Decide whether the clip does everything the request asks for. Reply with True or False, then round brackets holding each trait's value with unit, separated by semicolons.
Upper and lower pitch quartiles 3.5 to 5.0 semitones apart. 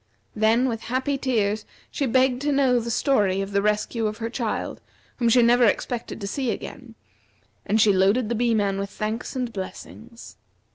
False (3.1 semitones)